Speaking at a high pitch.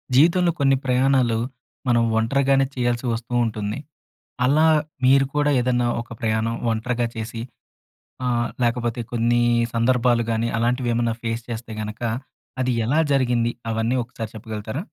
No: low, 120 Hz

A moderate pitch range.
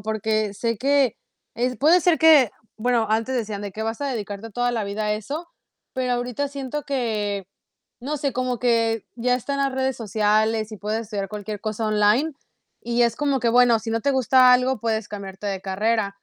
Yes: average, 3.3 semitones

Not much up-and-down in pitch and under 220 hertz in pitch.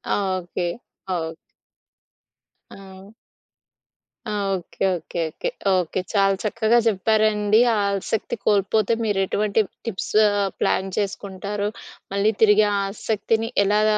Yes: narrow, 1.8 semitones; high, 205 Hz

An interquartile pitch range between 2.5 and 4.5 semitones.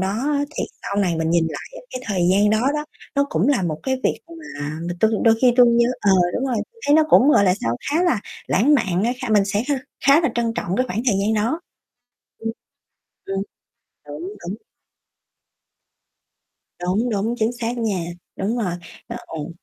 No: average, 5.0 semitones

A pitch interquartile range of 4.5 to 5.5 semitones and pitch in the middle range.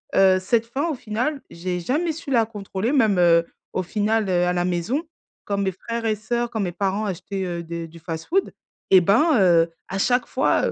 No: average, 4.8 semitones; high, 200 Hz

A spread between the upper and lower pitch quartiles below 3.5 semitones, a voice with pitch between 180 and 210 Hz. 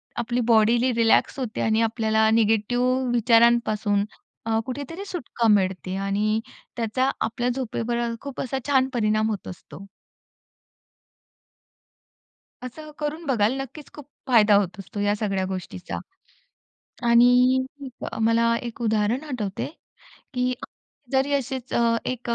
No: average, 3.1 semitones; high, 230 Hz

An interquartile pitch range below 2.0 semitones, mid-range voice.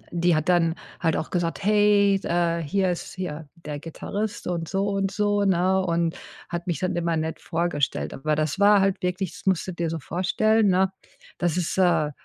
No: average, 2.8 semitones; medium, 175 Hz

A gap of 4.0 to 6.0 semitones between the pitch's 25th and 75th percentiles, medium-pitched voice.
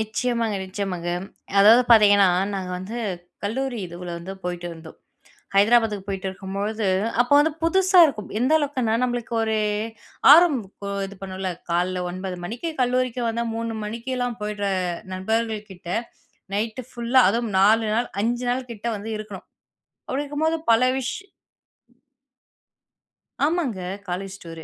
No: average, 4.3 semitones; high, 220 Hz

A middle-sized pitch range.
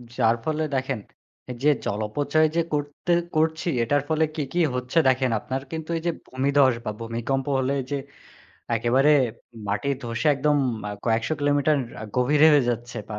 Yes: average, 3.8 semitones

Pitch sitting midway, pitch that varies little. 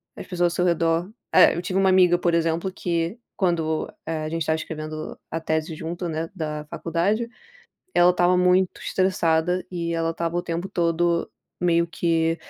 Yes: medium, 170 Hz; narrow, 1.5 semitones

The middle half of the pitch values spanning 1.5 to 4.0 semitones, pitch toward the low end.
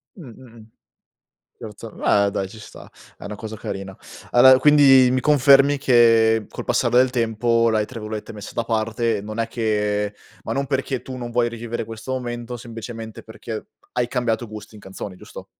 Yes: narrow, 2.5 semitones; low, 115 Hz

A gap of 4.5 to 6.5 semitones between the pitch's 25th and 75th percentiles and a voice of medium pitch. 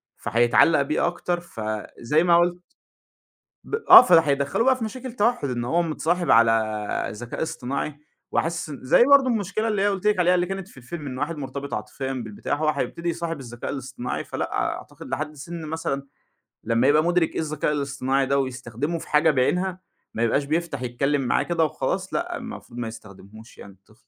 Yes: wide, 5.6 semitones; medium, 150 Hz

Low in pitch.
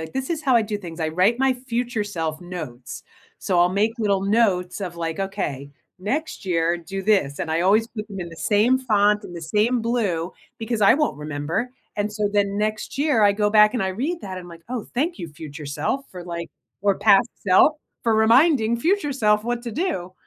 No: high, 205 Hz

